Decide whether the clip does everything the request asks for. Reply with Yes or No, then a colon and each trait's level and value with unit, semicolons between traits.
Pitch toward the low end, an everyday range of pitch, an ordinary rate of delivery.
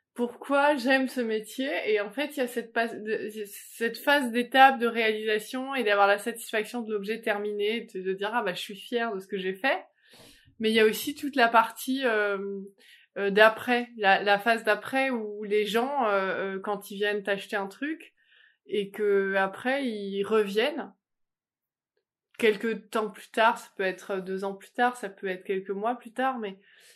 No: high, 220 Hz; average, 3.1 semitones; average, 185 wpm